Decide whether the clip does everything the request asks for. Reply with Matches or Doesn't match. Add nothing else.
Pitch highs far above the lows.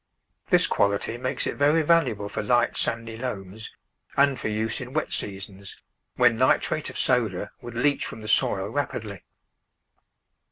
Doesn't match